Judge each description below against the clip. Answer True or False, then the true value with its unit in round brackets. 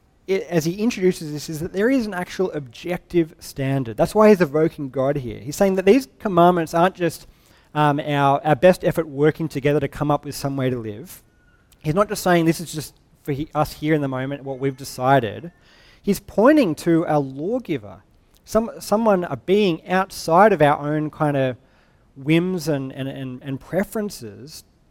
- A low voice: False (155 Hz)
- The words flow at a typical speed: True (190 wpm)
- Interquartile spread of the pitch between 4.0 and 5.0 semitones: True (4.7 semitones)